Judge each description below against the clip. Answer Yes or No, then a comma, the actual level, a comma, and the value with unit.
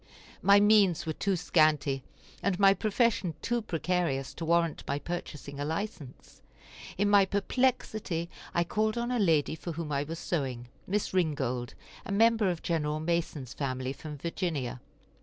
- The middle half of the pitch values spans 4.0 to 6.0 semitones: Yes, average, 5.3 semitones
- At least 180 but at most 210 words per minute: No, average, 155 wpm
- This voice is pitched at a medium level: Yes, medium, 170 Hz